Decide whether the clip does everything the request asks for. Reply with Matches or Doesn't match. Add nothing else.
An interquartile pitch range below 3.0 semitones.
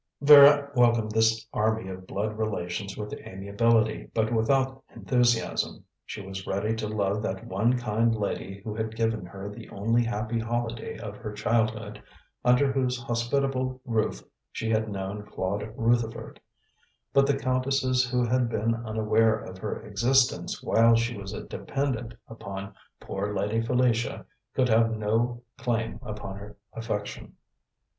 Matches